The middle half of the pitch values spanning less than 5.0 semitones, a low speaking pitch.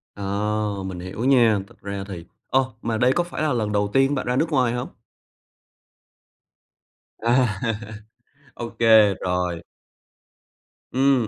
Yes: average, 4.3 semitones; low, 110 Hz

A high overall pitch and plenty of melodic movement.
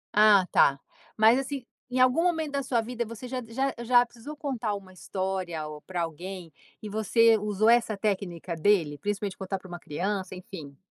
No: high, 210 Hz; average, 4.6 semitones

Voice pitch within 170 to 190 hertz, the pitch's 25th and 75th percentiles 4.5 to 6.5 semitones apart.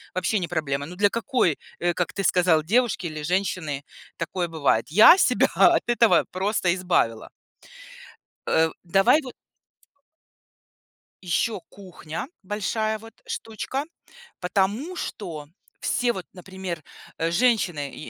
Yes: medium, 185 Hz; average, 4.9 semitones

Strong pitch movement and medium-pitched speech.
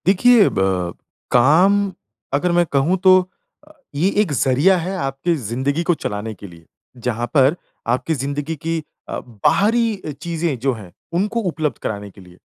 Yes: wide, 6.3 semitones; medium, 145 Hz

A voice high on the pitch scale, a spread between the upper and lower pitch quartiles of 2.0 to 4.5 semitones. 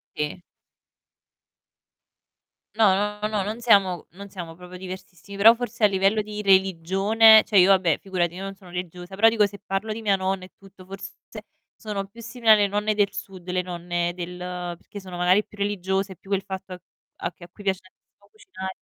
Yes: high, 195 Hz; narrow, 2.4 semitones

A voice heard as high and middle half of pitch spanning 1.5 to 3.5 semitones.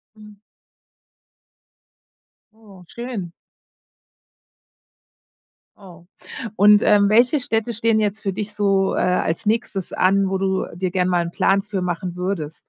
Yes: high, 195 Hz; average, 2.7 semitones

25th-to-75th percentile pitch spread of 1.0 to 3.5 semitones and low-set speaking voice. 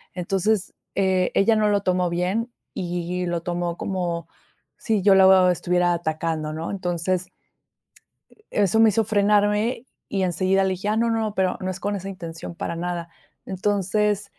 No: average, 2.7 semitones; medium, 185 Hz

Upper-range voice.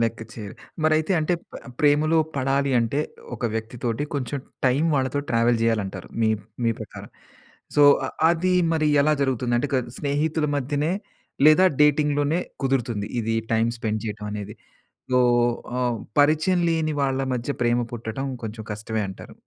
No: low, 130 Hz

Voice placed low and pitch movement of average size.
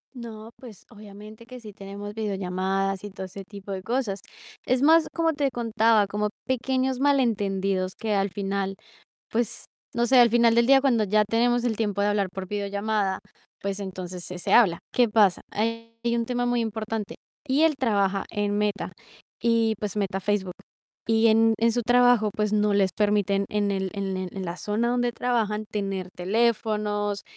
No: high, 210 Hz; average, 3.0 semitones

